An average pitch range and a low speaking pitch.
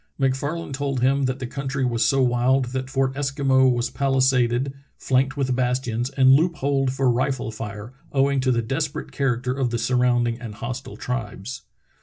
No: narrow, 1.9 semitones; low, 130 Hz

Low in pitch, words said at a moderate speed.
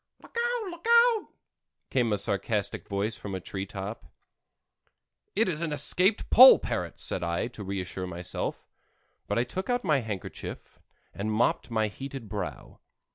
Yes: low, 110 Hz; average, 155 wpm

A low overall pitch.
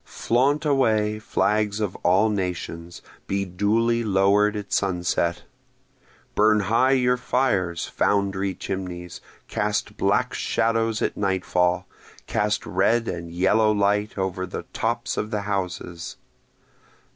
Yes: low, 100 Hz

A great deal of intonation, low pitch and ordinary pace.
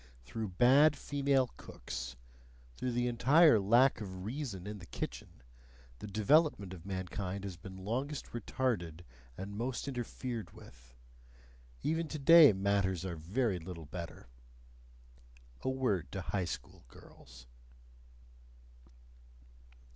No: wide, 6.0 semitones; low, 105 Hz; slow, 115 wpm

